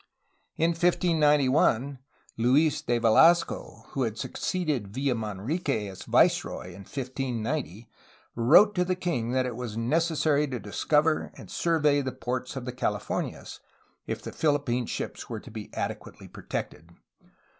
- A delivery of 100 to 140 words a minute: Yes, slow, 135 wpm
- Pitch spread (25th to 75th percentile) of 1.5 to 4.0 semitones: No, average, 5.0 semitones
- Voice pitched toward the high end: No, low, 130 Hz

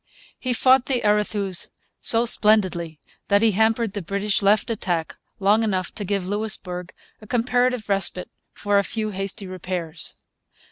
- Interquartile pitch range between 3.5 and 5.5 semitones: No, average, 3.0 semitones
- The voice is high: Yes, high, 205 Hz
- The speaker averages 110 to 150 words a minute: Yes, average, 145 wpm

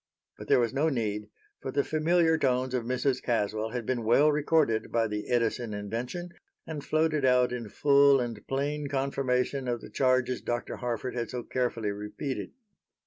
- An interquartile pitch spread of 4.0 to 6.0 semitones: No, average, 3.4 semitones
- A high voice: No, low, 125 Hz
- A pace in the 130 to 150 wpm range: No, average, 170 wpm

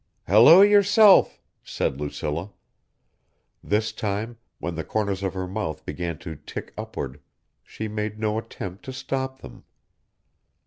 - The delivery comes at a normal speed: No, slow, 130 wpm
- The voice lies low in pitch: Yes, low, 105 Hz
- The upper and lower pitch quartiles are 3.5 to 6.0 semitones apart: Yes, wide, 5.4 semitones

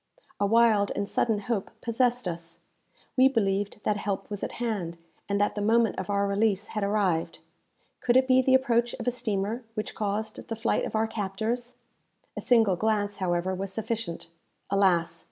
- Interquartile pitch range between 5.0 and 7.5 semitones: No, average, 2.9 semitones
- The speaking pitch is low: No, high, 210 Hz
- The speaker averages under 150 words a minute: No, average, 175 wpm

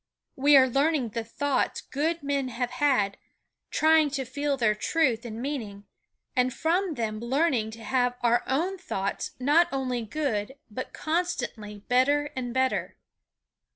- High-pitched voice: Yes, very high, 260 Hz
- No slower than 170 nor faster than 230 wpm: No, average, 145 wpm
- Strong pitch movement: No, average, 3.8 semitones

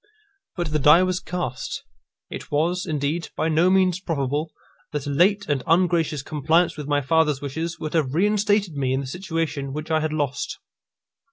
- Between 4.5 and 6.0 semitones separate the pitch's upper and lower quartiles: No, average, 3.5 semitones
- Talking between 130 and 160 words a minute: No, average, 175 wpm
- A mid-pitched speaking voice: Yes, medium, 160 Hz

